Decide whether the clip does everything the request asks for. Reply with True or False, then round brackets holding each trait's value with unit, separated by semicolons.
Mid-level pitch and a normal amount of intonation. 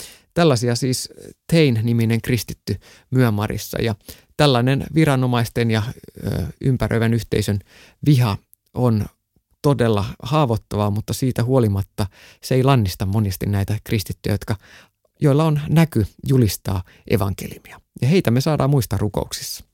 False (115 Hz; 4.2 semitones)